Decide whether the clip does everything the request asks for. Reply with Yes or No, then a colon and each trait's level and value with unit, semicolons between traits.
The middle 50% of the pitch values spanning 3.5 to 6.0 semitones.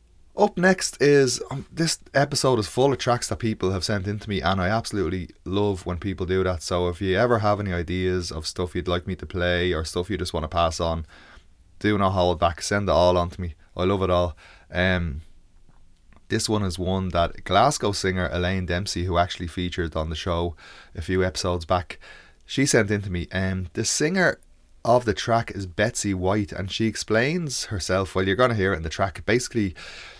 No: average, 3.1 semitones